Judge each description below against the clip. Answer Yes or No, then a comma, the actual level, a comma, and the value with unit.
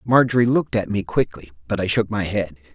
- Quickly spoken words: Yes, fast, 220 wpm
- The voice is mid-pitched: No, low, 105 Hz